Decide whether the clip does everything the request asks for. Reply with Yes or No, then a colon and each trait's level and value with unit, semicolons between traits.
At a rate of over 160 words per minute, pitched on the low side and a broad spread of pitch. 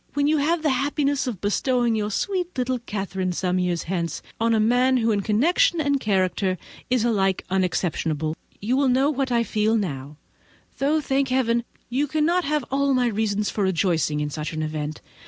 No: average, 185 wpm; high, 230 Hz; wide, 6.6 semitones